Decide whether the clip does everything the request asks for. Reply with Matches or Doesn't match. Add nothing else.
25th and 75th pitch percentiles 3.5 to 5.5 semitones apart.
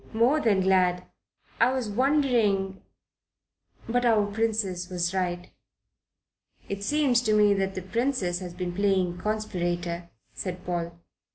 Matches